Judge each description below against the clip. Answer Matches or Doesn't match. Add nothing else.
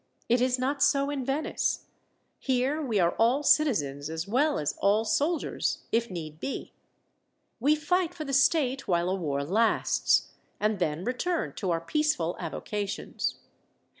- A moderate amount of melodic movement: Doesn't match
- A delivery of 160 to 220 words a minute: Doesn't match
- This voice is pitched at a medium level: Doesn't match